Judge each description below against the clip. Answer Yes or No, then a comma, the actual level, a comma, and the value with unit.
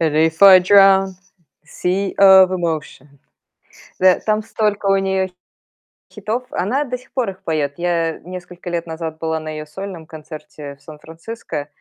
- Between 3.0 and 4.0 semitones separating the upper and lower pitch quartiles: Yes, average, 3.5 semitones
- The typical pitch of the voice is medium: Yes, medium, 180 Hz